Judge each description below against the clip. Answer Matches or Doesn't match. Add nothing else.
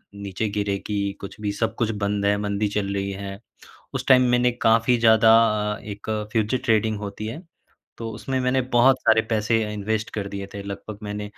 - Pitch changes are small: Matches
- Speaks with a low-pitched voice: Matches